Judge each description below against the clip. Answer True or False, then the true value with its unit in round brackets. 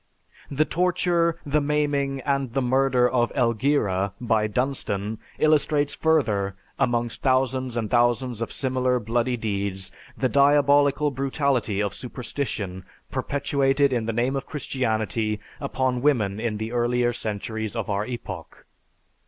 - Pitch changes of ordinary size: True (4.0 semitones)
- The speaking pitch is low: True (125 Hz)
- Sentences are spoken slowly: True (130 wpm)